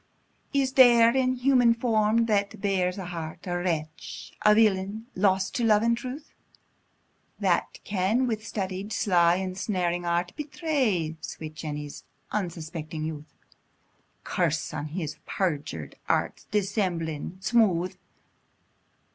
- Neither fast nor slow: No, slow, 115 wpm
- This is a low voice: No, high, 190 Hz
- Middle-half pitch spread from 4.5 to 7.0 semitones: Yes, average, 5.0 semitones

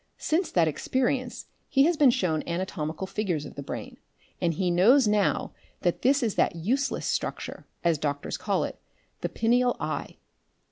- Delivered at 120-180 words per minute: Yes, average, 160 wpm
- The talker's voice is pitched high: Yes, high, 200 Hz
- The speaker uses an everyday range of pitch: No, wide, 7.3 semitones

